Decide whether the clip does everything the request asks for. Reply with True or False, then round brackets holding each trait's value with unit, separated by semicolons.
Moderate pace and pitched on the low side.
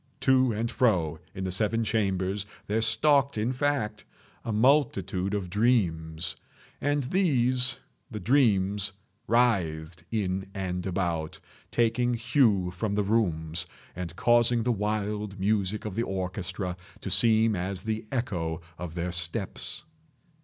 False (125 wpm; 105 Hz)